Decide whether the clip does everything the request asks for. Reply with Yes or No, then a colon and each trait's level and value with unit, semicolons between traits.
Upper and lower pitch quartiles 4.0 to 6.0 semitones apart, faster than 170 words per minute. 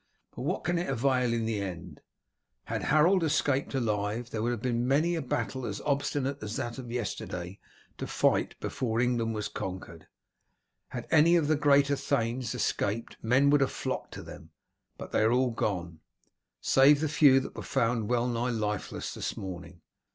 Yes: average, 4.3 semitones; average, 180 wpm